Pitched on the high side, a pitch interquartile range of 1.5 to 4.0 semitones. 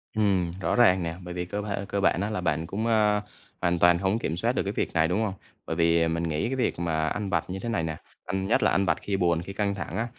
No: very low, 95 Hz; average, 3.5 semitones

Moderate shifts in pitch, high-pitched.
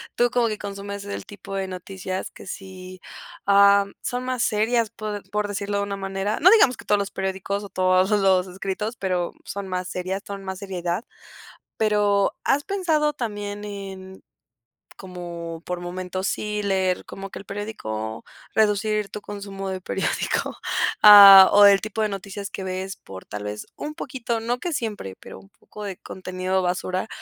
No: narrow, 2.0 semitones; high, 200 Hz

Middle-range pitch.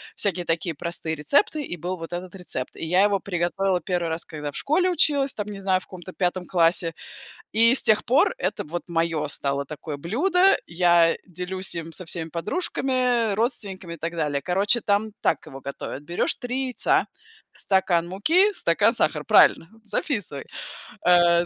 Yes: medium, 180 Hz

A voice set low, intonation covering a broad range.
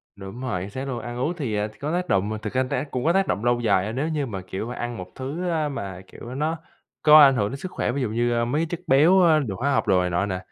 Yes: low, 125 Hz; wide, 6.4 semitones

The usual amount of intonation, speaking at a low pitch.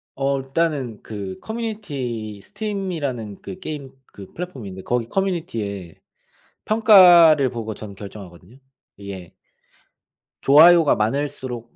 No: wide, 8.0 semitones; low, 130 Hz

